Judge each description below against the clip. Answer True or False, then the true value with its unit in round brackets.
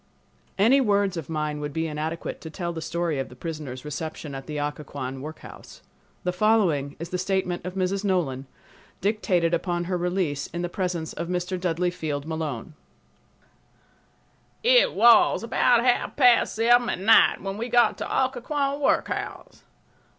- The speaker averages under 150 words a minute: False (160 wpm)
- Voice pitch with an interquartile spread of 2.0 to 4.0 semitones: False (4.9 semitones)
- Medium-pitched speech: True (175 Hz)